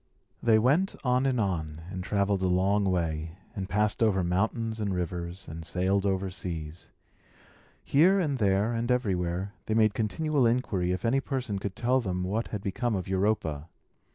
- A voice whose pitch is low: Yes, low, 100 Hz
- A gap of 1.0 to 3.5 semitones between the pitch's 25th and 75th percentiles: No, average, 4.1 semitones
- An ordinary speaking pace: Yes, average, 170 wpm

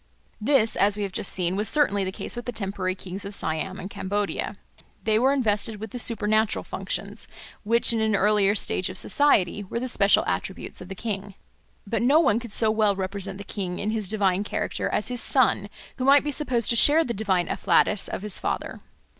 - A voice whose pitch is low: No, high, 210 Hz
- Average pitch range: Yes, average, 3.0 semitones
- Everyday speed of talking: No, fast, 210 wpm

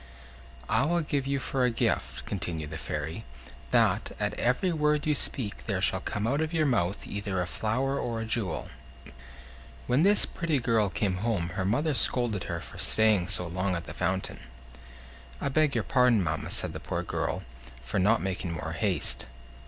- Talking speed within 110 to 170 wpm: No, average, 185 wpm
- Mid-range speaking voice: No, low, 110 Hz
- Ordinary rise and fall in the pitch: No, wide, 6.7 semitones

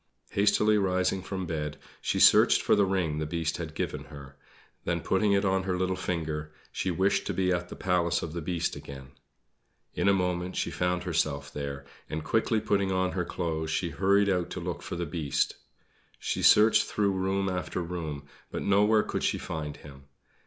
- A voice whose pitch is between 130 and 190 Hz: No, very low, 90 Hz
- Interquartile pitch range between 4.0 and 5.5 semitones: No, average, 3.3 semitones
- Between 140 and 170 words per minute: No, average, 190 wpm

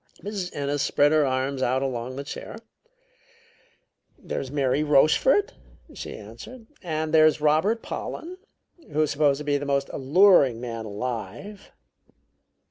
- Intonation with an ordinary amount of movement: Yes, average, 3.1 semitones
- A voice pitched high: No, medium, 145 Hz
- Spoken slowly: Yes, slow, 125 wpm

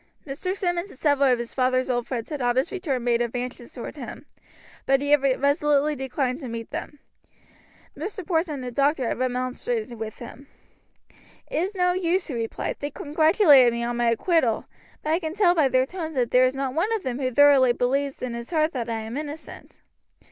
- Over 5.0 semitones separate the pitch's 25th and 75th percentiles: No, average, 4.2 semitones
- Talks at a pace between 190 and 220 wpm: Yes, fast, 205 wpm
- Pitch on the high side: Yes, very high, 270 Hz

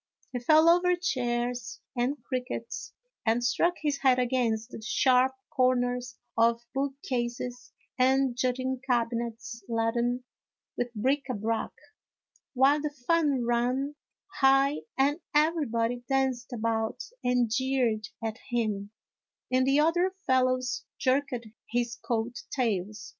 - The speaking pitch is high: Yes, very high, 250 Hz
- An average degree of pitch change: No, narrow, 2.2 semitones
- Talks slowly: Yes, slow, 115 wpm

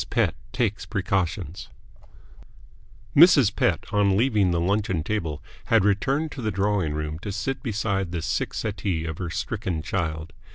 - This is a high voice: No, low, 100 Hz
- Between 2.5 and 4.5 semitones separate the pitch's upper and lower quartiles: Yes, average, 4.1 semitones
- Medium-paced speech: Yes, average, 150 wpm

